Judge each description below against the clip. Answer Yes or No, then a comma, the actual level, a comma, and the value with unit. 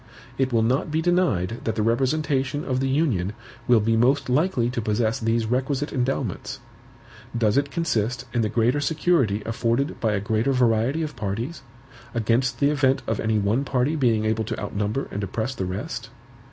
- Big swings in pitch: No, average, 3.9 semitones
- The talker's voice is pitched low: Yes, low, 120 Hz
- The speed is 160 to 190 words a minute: Yes, average, 180 wpm